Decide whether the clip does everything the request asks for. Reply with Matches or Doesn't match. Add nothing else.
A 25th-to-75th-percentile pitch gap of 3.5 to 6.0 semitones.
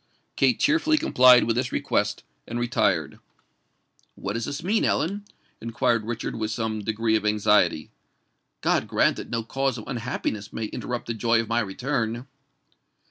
Doesn't match